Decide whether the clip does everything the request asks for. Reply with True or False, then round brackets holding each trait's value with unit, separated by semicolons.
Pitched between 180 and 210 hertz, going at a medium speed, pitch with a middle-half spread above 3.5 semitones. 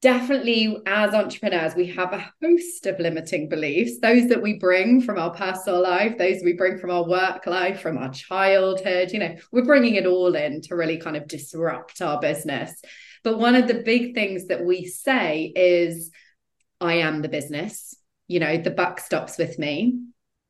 True (185 Hz; 185 wpm; 4.2 semitones)